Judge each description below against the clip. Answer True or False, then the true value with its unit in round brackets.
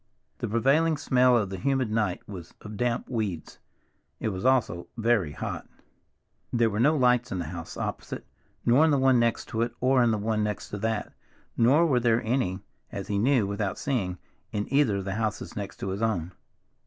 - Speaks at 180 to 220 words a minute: True (200 wpm)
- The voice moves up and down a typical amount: True (3.9 semitones)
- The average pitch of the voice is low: True (115 Hz)